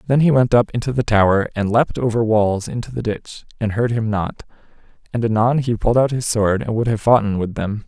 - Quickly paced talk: Yes, fast, 235 wpm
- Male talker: Yes, male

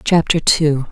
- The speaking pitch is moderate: Yes, medium, 155 Hz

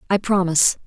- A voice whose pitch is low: No, medium, 185 Hz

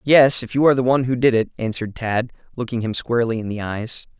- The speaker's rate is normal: No, fast, 245 wpm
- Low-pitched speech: Yes, low, 120 Hz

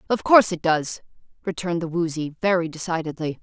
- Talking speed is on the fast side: No, average, 160 wpm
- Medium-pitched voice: Yes, medium, 170 Hz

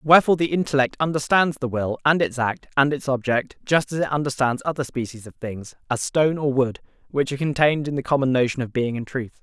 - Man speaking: Yes, male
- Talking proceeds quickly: Yes, fast, 225 wpm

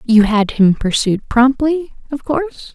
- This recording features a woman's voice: Yes, female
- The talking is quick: No, average, 155 wpm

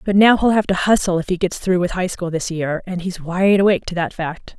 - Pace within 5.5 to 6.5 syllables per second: Yes, 5.6 syllables/s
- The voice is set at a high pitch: No, medium, 180 Hz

